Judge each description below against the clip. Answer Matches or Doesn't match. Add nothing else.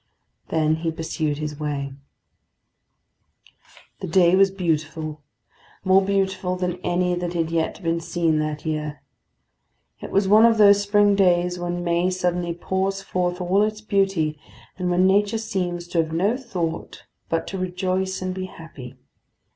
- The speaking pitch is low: Doesn't match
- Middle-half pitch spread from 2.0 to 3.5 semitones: Matches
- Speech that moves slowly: Doesn't match